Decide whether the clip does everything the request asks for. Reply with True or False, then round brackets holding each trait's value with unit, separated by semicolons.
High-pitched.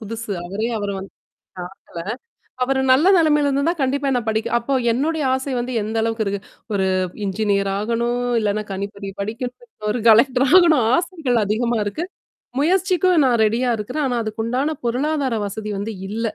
True (235 Hz)